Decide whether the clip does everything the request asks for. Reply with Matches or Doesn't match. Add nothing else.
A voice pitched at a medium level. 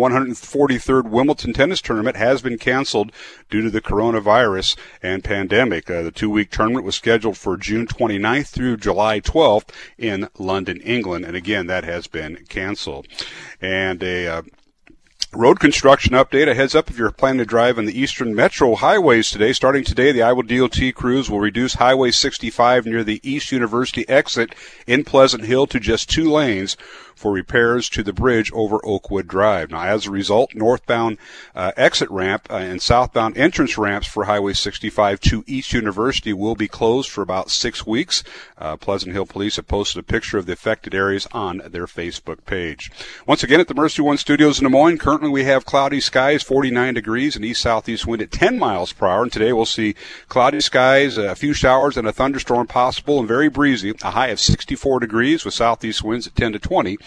Doesn't match